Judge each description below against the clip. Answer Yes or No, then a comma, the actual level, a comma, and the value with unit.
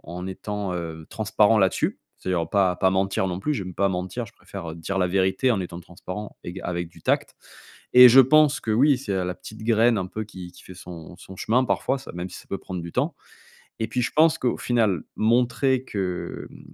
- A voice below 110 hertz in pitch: Yes, very low, 95 Hz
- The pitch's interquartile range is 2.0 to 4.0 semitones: No, average, 4.4 semitones